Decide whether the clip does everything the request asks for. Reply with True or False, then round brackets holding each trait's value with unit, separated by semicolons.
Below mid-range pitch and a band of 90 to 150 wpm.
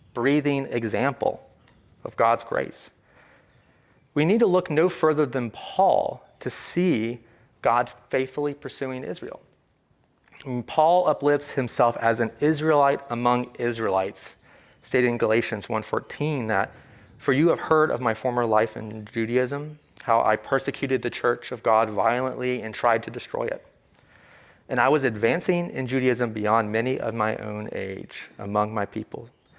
True (125 Hz; 145 wpm)